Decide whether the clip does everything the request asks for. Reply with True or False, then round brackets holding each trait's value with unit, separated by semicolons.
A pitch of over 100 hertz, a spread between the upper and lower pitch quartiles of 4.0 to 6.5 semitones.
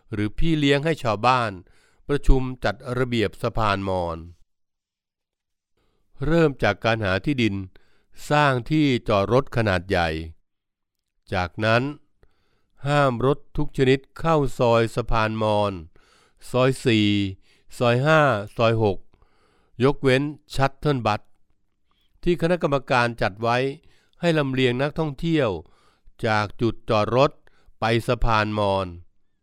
True (115 Hz; 5.2 semitones)